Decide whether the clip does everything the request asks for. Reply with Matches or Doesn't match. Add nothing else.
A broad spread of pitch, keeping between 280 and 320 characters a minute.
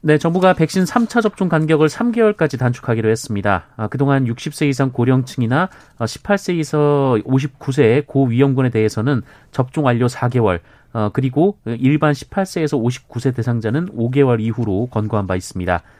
Doesn't match